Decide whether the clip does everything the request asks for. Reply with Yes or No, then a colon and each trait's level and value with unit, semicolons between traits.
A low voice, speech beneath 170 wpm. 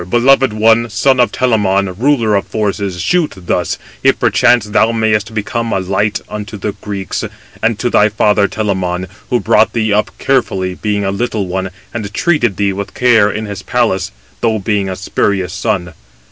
No: low, 105 Hz; average, 180 wpm